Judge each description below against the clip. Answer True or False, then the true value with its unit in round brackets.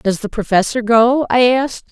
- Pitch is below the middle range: False (235 Hz)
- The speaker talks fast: False (190 wpm)